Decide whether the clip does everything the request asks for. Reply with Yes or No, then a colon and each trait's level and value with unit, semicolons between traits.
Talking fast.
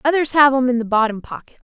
Yes: fast, 250 wpm